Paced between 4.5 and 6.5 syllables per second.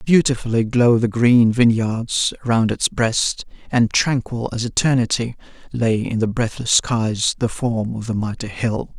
No: 4.2 syllables/s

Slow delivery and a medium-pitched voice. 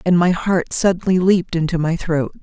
No: average, 200 wpm; medium, 175 Hz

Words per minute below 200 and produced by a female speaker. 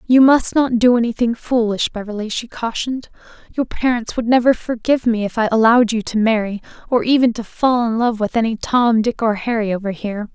No: fast, 205 wpm; female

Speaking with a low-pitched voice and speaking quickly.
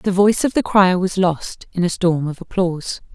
No: medium, 185 Hz; fast, 230 wpm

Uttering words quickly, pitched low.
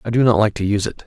Yes: fast, 395 wpm; low, 110 Hz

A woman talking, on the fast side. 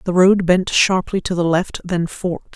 Yes: female; fast, 210 wpm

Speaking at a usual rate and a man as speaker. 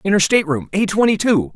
Yes: average, 195 wpm; male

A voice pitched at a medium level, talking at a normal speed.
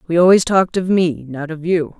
No: medium, 170 Hz; fast, 240 wpm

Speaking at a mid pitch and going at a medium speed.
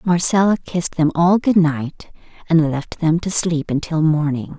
Yes: medium, 165 Hz; average, 170 wpm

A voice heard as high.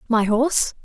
Yes: high, 235 Hz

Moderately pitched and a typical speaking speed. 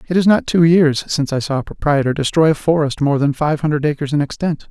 No: medium, 150 Hz; fast, 255 wpm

